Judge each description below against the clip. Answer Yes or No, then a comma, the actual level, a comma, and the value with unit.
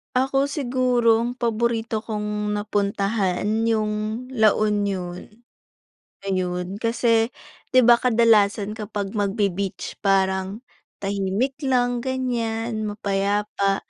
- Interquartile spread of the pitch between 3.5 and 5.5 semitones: No, average, 2.9 semitones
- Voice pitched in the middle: No, high, 215 Hz